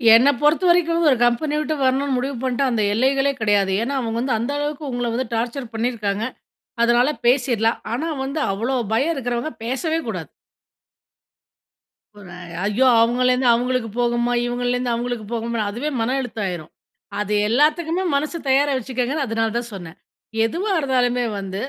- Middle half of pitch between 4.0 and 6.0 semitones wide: No, average, 3.3 semitones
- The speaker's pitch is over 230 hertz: Yes, high, 245 Hz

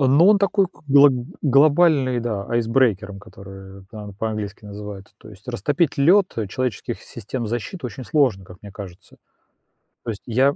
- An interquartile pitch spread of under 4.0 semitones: No, wide, 5.4 semitones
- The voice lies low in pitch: Yes, low, 115 Hz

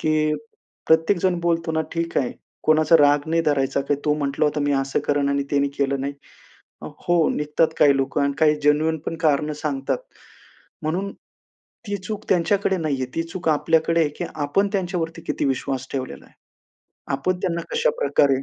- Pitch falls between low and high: Yes, medium, 155 Hz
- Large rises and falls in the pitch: No, average, 2.9 semitones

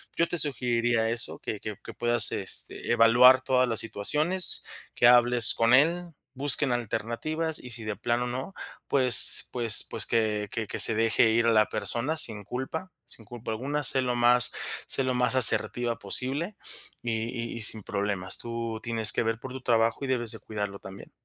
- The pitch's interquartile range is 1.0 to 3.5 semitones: Yes, narrow, 2.5 semitones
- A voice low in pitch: Yes, low, 120 Hz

